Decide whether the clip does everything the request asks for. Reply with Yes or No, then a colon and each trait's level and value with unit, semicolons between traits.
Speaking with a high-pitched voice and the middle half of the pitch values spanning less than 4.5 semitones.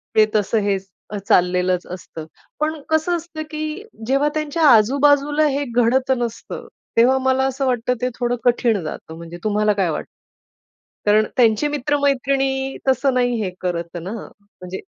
No: high, 245 Hz; wide, 5.5 semitones